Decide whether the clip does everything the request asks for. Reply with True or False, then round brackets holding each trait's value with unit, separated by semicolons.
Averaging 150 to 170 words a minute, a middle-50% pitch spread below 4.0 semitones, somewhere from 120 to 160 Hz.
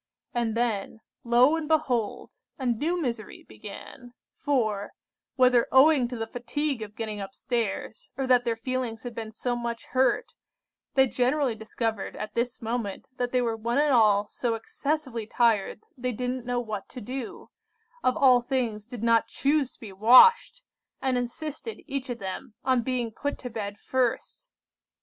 False (160 wpm; 2.7 semitones; 245 Hz)